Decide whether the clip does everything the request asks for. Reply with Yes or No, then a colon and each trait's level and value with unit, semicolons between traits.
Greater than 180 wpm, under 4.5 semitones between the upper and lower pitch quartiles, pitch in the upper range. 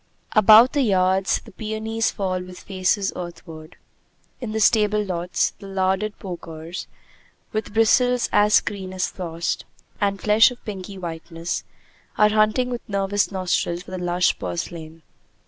No: average, 140 wpm; average, 3.1 semitones; high, 195 Hz